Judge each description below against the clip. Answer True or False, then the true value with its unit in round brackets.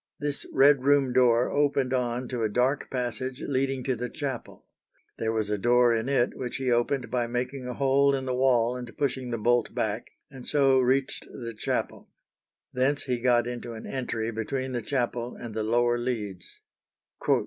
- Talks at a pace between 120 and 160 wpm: False (180 wpm)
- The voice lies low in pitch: True (125 Hz)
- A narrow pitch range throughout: True (2.0 semitones)